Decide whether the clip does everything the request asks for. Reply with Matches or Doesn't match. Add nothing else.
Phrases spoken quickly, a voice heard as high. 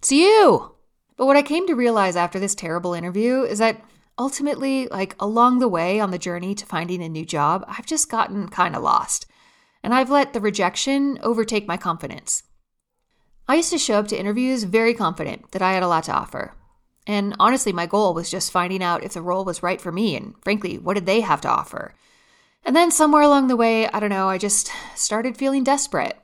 Matches